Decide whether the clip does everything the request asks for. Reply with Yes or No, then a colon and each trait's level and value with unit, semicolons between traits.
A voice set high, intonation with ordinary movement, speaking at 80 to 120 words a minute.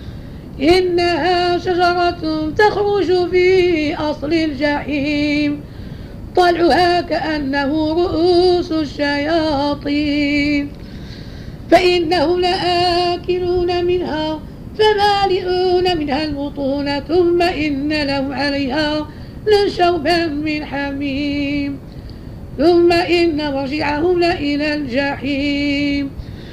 No: very high, 320 Hz; average, 3.6 semitones; slow, 65 wpm